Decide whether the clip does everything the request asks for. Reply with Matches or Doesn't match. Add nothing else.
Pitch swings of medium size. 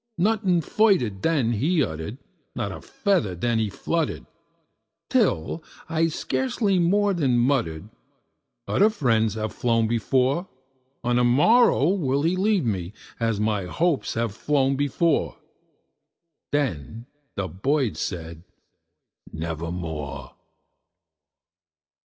Doesn't match